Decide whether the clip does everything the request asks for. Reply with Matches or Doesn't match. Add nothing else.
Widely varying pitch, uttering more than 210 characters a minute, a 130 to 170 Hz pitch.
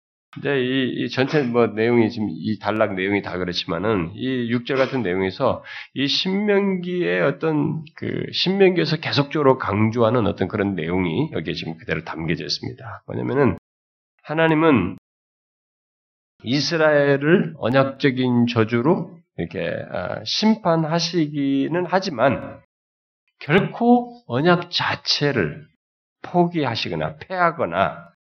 Matches